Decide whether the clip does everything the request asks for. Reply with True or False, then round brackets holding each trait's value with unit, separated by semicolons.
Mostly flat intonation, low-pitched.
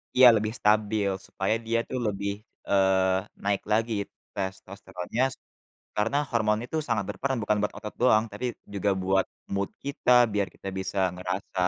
True (2.3 semitones; 100 Hz)